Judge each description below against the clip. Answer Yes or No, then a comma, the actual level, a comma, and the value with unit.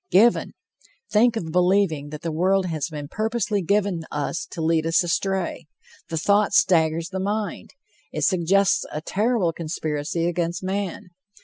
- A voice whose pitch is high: No, medium, 180 Hz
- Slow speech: No, average, 145 wpm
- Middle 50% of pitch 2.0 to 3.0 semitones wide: No, average, 3.7 semitones